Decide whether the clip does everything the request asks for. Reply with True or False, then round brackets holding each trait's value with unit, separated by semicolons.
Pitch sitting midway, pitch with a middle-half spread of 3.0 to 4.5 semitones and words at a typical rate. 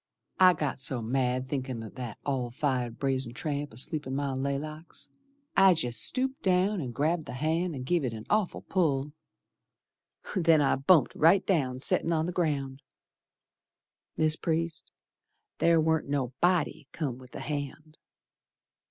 True (145 Hz; 4.1 semitones; 150 wpm)